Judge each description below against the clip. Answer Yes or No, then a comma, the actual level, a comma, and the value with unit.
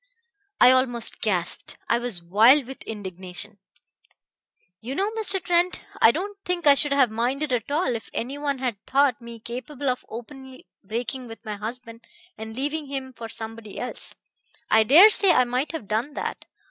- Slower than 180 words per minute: Yes, average, 170 wpm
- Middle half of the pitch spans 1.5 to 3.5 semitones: No, average, 4.2 semitones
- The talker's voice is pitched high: Yes, very high, 250 Hz